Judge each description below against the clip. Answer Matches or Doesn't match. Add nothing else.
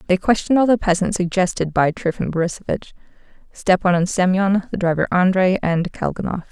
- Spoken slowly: Doesn't match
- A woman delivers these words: Matches